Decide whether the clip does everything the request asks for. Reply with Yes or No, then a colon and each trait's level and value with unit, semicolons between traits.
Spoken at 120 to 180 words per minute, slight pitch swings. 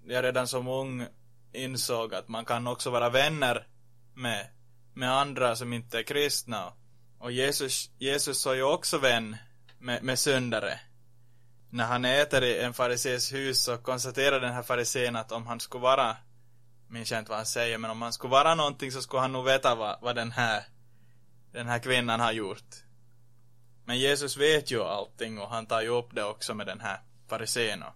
No: average, 190 wpm; narrow, 1.6 semitones